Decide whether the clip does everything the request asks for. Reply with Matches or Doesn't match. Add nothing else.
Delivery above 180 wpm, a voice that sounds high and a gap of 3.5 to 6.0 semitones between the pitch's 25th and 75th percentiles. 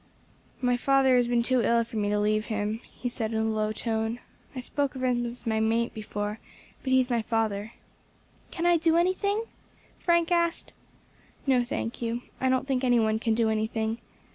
Doesn't match